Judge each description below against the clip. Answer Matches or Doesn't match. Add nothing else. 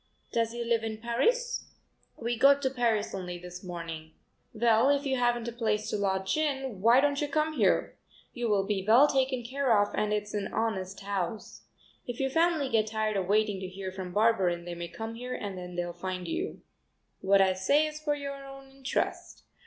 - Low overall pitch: Doesn't match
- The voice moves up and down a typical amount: Doesn't match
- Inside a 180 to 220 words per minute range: Matches